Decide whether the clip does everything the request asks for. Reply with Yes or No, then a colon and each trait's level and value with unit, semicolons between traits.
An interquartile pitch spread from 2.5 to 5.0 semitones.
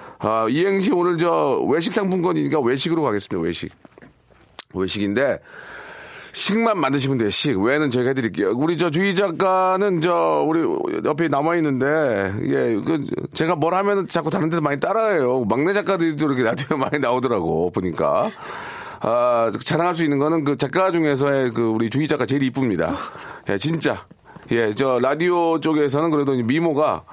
No: wide, 5.4 semitones